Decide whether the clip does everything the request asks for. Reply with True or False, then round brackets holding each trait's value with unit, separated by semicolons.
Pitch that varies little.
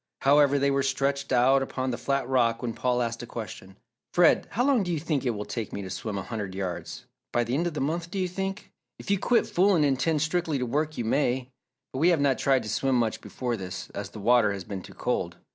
False (5.0 semitones)